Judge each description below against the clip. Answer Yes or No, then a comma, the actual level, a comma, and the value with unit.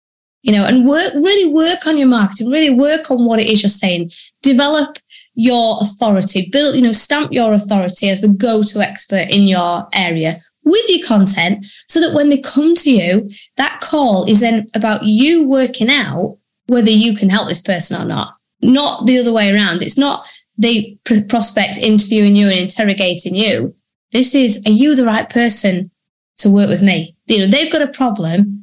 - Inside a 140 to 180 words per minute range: No, average, 190 wpm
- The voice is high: Yes, high, 220 Hz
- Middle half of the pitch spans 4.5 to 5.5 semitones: Yes, average, 5.1 semitones